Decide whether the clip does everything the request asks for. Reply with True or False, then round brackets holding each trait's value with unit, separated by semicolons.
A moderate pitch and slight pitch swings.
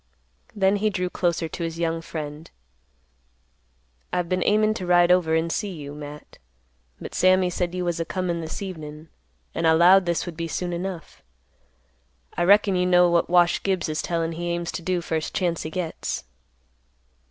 True (175 Hz; 1.9 semitones)